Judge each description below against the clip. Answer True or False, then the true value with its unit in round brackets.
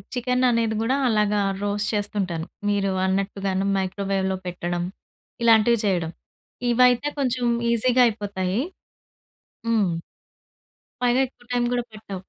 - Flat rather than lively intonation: False (3.9 semitones)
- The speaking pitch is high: True (210 Hz)